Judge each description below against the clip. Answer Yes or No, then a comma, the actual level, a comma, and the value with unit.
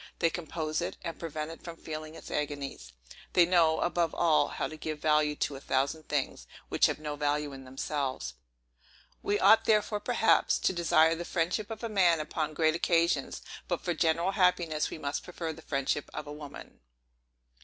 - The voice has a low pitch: No, medium, 160 Hz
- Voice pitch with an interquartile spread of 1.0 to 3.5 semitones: Yes, narrow, 2.6 semitones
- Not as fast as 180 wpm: No, average, 185 wpm